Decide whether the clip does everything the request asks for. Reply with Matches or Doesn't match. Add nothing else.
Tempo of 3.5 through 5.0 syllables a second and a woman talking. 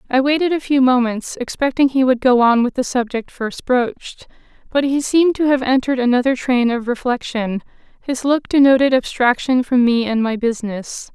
Doesn't match